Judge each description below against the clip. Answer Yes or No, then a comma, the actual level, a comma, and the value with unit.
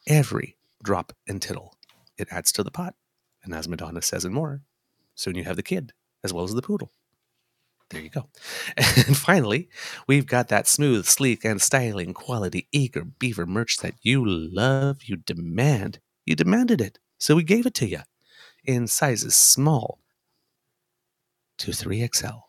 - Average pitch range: No, wide, 6.1 semitones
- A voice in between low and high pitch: No, low, 125 Hz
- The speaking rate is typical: Yes, average, 160 wpm